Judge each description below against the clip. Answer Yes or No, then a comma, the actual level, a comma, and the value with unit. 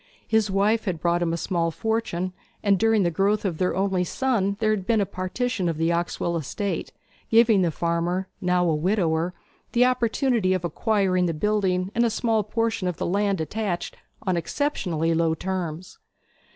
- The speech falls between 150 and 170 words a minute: No, average, 180 wpm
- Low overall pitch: No, medium, 185 Hz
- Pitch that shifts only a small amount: No, average, 4.0 semitones